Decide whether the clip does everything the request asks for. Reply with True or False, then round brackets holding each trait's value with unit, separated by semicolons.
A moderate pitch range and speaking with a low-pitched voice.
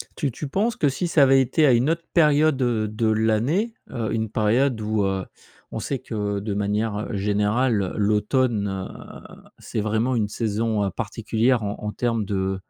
True (4.0 semitones; 110 Hz)